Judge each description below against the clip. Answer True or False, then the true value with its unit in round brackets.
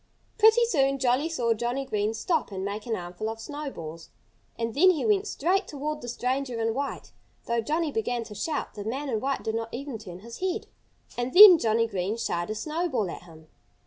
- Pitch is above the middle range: True (240 Hz)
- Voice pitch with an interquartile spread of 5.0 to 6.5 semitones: True (5.5 semitones)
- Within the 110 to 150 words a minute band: False (205 wpm)